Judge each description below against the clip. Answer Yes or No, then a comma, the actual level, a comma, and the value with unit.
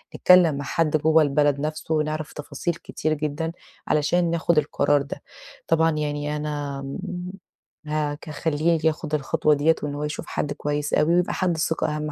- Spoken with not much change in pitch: Yes, narrow, 1.7 semitones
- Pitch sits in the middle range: Yes, medium, 150 Hz